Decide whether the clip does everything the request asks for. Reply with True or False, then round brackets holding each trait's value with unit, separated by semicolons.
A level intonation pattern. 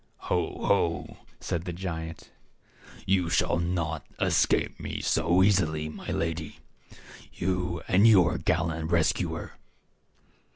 True (1.9 semitones)